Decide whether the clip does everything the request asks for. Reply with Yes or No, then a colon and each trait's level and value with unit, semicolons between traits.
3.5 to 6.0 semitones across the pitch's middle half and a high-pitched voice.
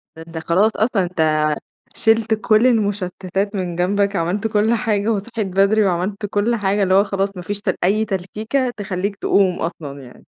No: average, 2.8 semitones; high, 200 Hz